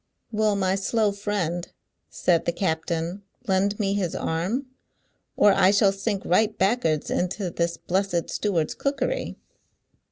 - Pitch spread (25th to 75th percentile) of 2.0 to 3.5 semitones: Yes, average, 3.1 semitones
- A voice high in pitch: Yes, high, 195 Hz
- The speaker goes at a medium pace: No, slow, 130 wpm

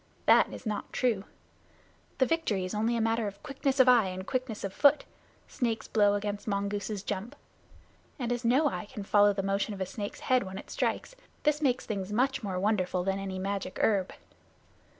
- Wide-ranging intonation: No, average, 4.0 semitones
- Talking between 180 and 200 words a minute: Yes, average, 190 wpm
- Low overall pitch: No, high, 210 Hz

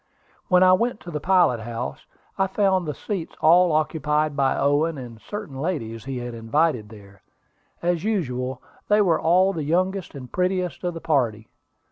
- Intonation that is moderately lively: No, wide, 6.3 semitones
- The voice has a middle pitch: Yes, medium, 155 Hz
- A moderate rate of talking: Yes, average, 170 wpm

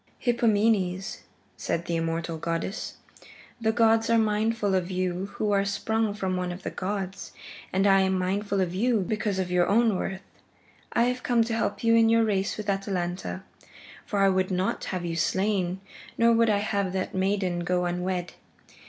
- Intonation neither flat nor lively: Yes, average, 3.0 semitones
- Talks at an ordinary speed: Yes, average, 180 wpm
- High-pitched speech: Yes, high, 195 Hz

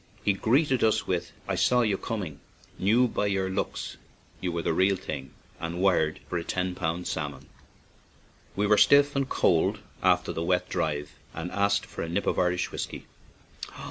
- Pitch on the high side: No, very low, 95 Hz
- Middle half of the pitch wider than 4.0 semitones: No, average, 3.7 semitones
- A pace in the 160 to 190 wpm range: Yes, average, 175 wpm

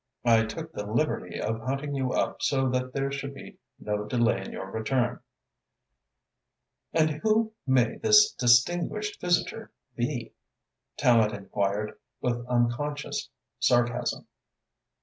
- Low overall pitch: Yes, low, 125 Hz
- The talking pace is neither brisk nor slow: No, slow, 120 wpm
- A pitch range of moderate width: Yes, average, 4.6 semitones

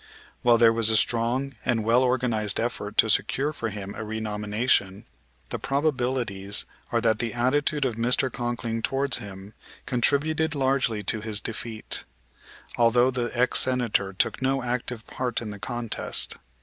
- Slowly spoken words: No, average, 150 wpm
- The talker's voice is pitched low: Yes, low, 120 Hz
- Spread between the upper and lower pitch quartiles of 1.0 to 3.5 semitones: Yes, average, 2.9 semitones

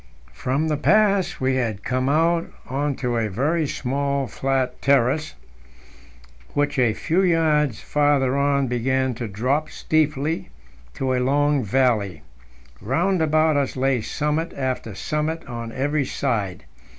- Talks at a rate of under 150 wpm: Yes, slow, 135 wpm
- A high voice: No, low, 135 Hz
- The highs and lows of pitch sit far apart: No, average, 3.3 semitones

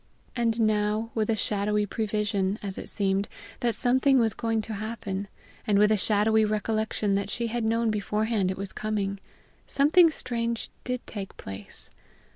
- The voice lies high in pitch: Yes, high, 215 Hz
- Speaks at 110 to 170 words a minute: Yes, average, 160 wpm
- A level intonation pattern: Yes, narrow, 2.2 semitones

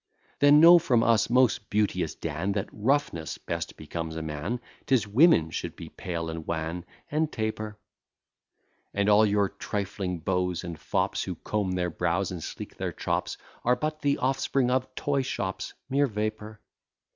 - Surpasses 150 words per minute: Yes, average, 160 wpm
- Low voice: Yes, low, 105 Hz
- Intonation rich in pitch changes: Yes, wide, 6.4 semitones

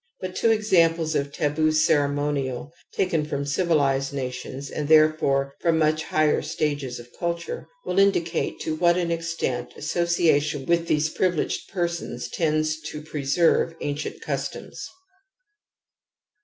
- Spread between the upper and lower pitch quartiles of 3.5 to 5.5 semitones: No, average, 2.9 semitones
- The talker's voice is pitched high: No, medium, 155 Hz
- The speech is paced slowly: Yes, slow, 125 wpm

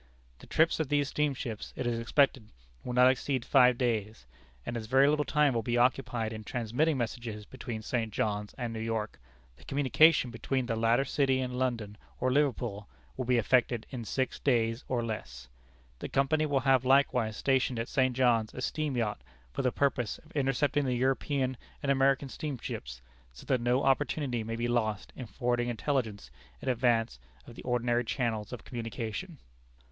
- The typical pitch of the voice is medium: No, low, 125 Hz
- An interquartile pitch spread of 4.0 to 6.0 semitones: No, average, 2.9 semitones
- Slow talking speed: No, average, 175 wpm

